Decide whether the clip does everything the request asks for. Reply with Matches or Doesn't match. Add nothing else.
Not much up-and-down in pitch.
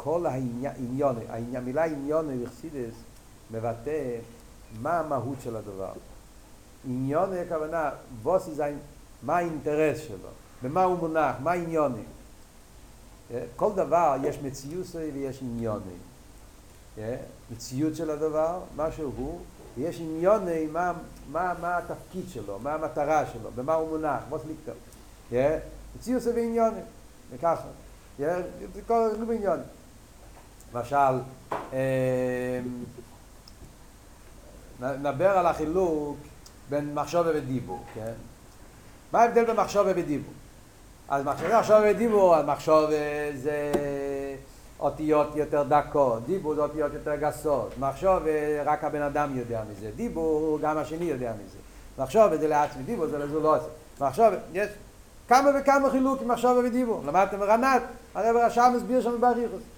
Doesn't match